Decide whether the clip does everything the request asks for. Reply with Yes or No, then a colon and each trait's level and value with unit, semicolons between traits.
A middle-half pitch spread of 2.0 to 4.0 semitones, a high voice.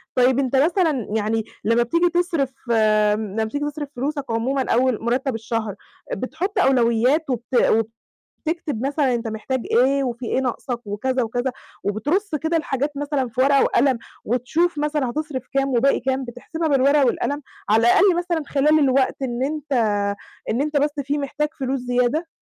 Yes: average, 3.7 semitones; very high, 265 Hz